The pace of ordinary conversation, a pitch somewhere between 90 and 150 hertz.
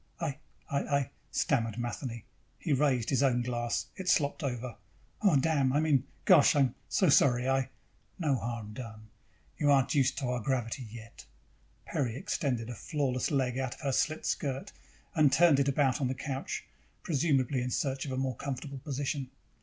Yes: average, 175 wpm; low, 135 Hz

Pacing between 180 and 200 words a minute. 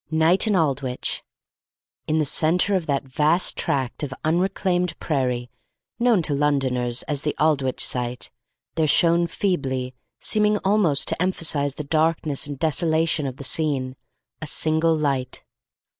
No: average, 140 wpm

